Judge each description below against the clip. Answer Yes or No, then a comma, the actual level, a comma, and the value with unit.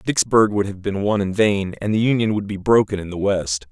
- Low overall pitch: Yes, low, 100 Hz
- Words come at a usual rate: No, fast, 260 wpm